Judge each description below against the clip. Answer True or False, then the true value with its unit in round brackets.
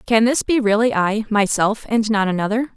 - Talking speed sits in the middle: True (195 wpm)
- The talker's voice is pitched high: True (220 Hz)